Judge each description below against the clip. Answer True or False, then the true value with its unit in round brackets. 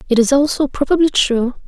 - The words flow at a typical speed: True (180 wpm)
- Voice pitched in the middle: False (270 Hz)